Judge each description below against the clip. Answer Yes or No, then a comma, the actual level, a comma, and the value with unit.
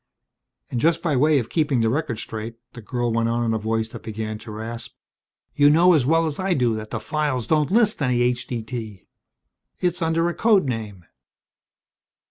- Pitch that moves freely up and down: Yes, wide, 5.8 semitones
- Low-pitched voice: Yes, low, 125 Hz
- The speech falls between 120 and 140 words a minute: No, average, 190 wpm